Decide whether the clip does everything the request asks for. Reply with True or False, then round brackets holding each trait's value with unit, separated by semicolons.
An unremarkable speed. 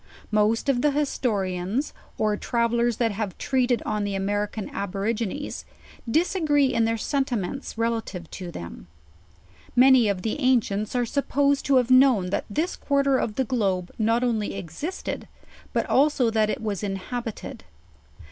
True (145 wpm)